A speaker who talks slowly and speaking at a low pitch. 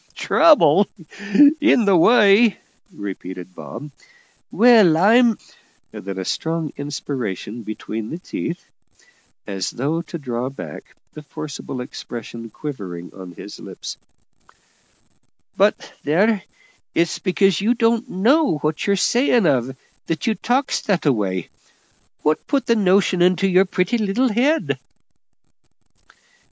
No: slow, 120 wpm; medium, 170 Hz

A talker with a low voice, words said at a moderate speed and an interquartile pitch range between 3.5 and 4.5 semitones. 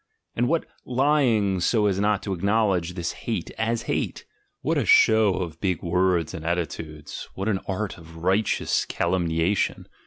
Yes: very low, 95 Hz; average, 160 wpm; average, 4.0 semitones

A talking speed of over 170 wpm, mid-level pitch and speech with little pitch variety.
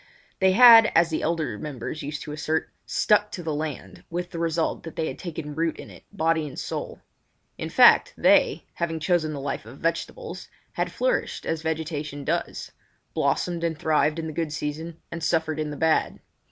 Yes: average, 185 wpm; medium, 160 Hz; narrow, 1.8 semitones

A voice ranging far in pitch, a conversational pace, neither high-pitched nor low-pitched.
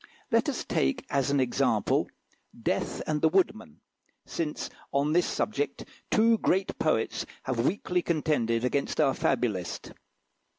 No: wide, 6.2 semitones; slow, 130 wpm; medium, 145 Hz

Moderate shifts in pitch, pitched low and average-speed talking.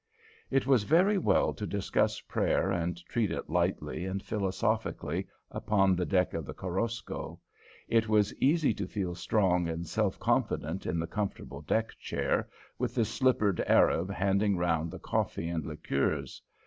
Yes: average, 4.2 semitones; very low, 95 Hz; average, 155 wpm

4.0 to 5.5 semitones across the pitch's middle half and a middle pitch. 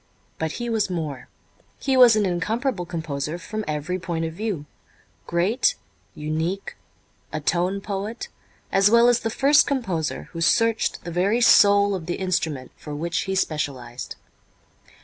Yes: average, 5.2 semitones; medium, 180 Hz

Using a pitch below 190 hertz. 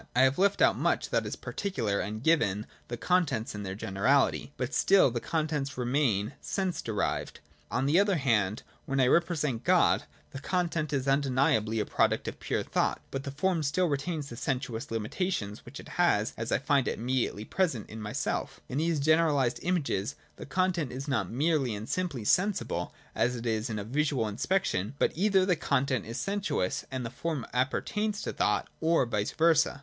Yes: low, 135 Hz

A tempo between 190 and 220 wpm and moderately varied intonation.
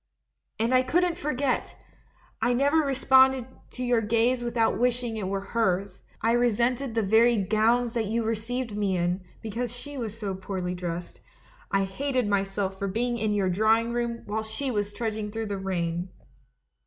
No: average, 165 wpm; average, 3.6 semitones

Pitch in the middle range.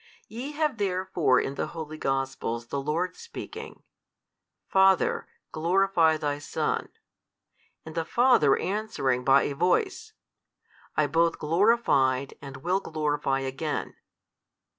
Yes: medium, 160 Hz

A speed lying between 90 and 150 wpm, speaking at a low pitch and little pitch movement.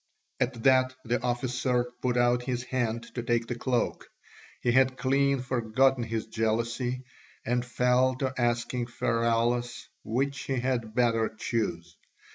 Yes: slow, 135 wpm; low, 120 Hz; narrow, 1.6 semitones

